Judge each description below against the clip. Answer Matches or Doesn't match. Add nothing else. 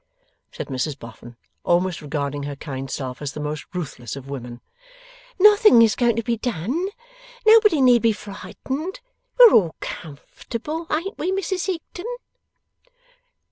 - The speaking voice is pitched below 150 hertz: Doesn't match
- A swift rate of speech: Doesn't match